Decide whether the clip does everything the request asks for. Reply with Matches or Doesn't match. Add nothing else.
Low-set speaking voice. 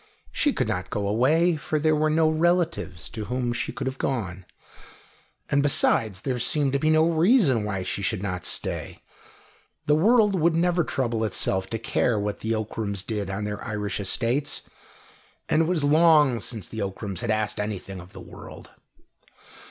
Matches